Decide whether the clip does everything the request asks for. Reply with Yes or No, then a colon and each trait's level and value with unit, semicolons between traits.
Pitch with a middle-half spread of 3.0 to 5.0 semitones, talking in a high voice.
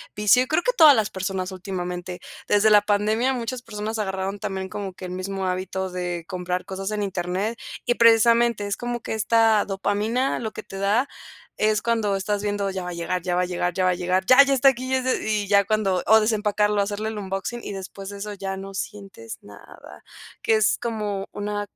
No: narrow, 2.5 semitones; high, 205 Hz